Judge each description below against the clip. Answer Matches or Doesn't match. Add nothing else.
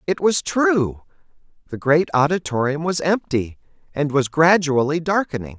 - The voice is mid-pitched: Matches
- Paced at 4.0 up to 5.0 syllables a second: Matches